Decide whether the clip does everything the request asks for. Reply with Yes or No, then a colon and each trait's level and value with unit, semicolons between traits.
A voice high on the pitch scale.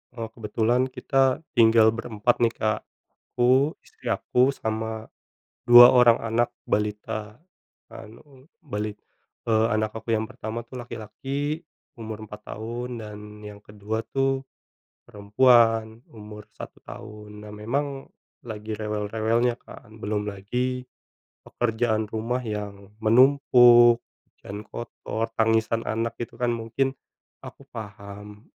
No: low, 115 Hz